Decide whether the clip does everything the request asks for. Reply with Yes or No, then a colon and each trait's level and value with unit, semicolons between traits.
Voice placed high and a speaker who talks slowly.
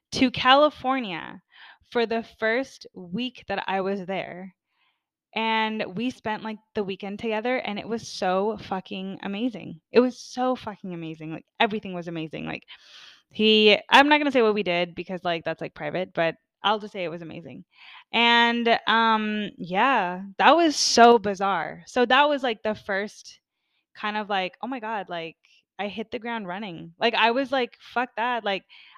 No: high, 215 Hz; average, 180 wpm